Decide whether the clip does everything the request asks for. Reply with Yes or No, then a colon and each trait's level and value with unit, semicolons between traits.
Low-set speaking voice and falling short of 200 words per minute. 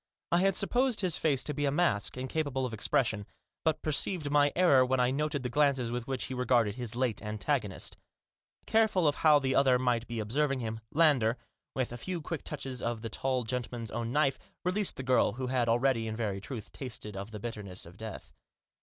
No: low, 130 Hz; fast, 205 wpm